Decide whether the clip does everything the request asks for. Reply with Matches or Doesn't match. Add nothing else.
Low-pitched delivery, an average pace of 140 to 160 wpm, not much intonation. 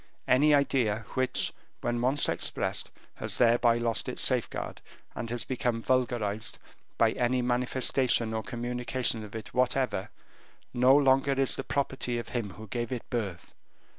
Matches